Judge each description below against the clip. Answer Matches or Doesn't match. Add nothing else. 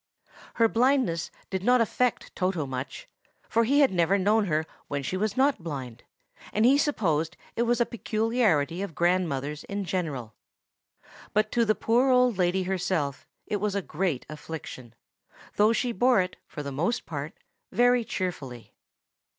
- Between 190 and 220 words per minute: Doesn't match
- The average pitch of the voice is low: Doesn't match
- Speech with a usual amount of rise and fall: Doesn't match